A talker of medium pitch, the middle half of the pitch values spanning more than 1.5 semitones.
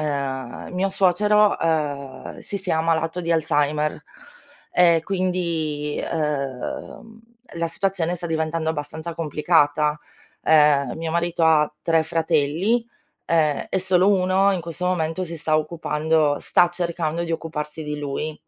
Yes: medium, 160 Hz; average, 2.7 semitones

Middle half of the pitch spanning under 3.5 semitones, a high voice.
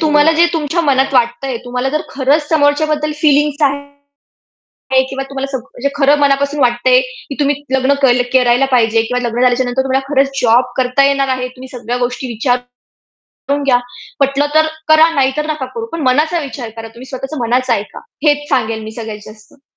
Yes: average, 2.8 semitones; very high, 270 Hz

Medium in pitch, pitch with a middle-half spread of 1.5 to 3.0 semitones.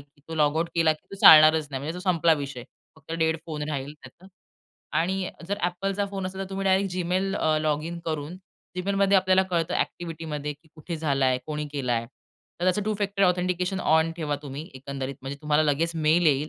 No: medium, 160 Hz; average, 3.7 semitones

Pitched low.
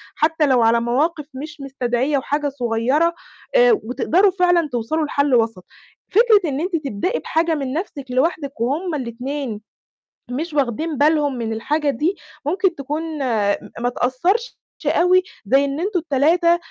No: very high, 290 Hz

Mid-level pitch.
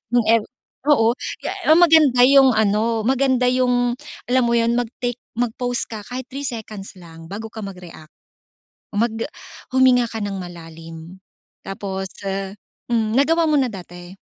No: high, 230 Hz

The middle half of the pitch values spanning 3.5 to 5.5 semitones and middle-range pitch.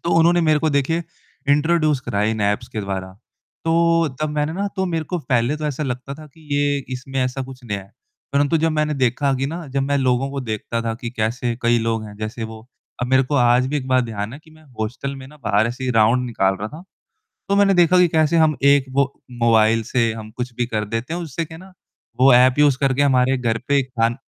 No: average, 4.6 semitones; low, 130 Hz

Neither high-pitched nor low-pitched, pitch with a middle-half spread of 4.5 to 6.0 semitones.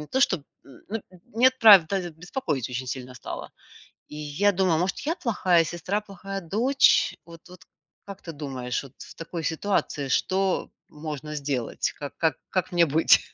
Yes: medium, 170 Hz; average, 5.0 semitones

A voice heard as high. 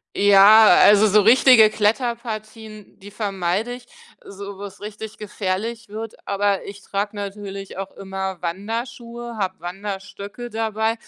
Yes: high, 210 Hz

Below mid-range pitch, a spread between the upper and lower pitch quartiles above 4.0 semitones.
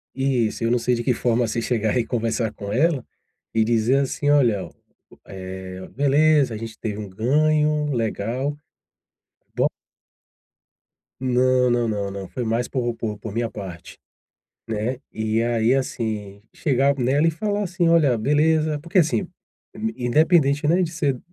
Yes: low, 125 Hz; average, 4.8 semitones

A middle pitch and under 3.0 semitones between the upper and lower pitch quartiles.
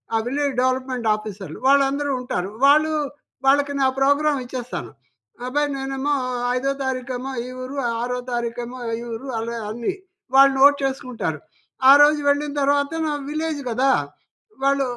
No: very high, 270 Hz; narrow, 2.5 semitones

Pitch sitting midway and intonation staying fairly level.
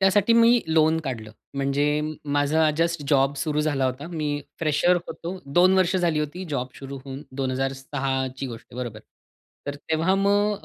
No: medium, 150 Hz; average, 4.3 semitones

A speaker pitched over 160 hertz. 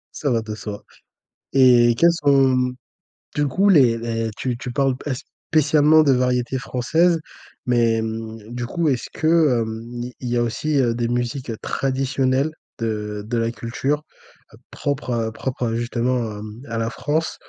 No: low, 125 Hz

